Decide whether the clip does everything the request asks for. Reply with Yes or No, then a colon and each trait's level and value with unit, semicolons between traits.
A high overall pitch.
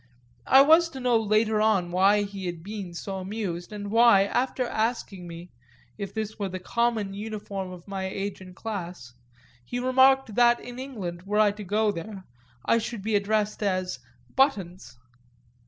Yes: high, 205 Hz